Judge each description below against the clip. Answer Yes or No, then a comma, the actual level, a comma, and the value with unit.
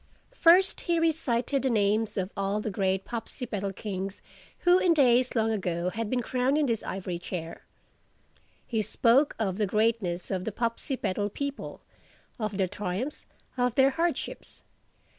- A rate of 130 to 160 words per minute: Yes, average, 150 wpm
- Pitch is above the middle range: Yes, high, 225 Hz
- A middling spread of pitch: Yes, average, 4.9 semitones